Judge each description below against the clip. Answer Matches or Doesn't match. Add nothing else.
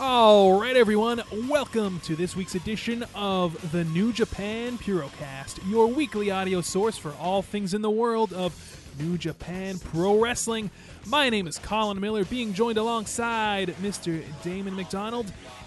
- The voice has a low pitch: Doesn't match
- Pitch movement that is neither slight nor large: Matches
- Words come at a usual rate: Matches